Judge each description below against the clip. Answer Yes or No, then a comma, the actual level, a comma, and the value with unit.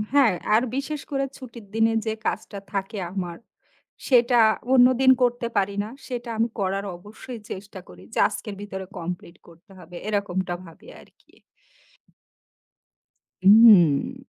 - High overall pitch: Yes, high, 210 Hz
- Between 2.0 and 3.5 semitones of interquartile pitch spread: No, average, 4.3 semitones